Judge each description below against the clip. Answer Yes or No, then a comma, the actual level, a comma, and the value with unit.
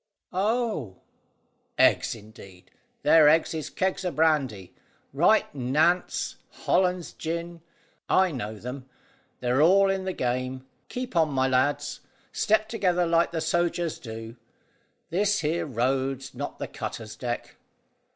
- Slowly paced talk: Yes, slow, 125 wpm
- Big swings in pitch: Yes, wide, 5.7 semitones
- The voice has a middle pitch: Yes, medium, 155 Hz